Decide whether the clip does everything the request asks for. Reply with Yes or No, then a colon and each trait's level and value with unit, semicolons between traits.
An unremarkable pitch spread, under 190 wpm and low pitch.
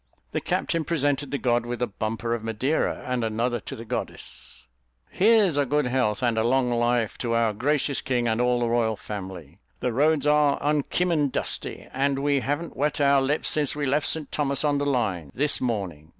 No: average, 3.9 semitones; average, 195 wpm; low, 130 Hz